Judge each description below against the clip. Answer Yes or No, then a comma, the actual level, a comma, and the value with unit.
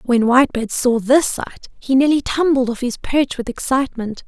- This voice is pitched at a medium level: No, very high, 255 Hz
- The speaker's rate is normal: Yes, average, 185 wpm